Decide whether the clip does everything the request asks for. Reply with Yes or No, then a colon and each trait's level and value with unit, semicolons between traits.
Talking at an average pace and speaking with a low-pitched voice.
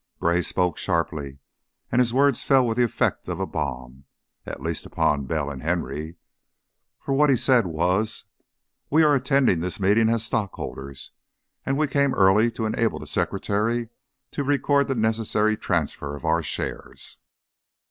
Yes: average, 155 wpm; low, 110 Hz